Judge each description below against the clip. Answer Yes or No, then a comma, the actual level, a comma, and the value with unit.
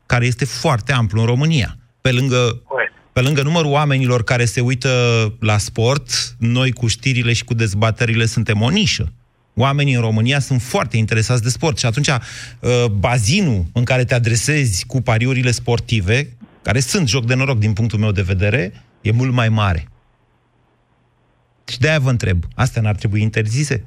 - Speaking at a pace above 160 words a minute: Yes, fast, 170 wpm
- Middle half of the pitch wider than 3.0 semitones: No, narrow, 2.5 semitones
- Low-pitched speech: Yes, low, 120 Hz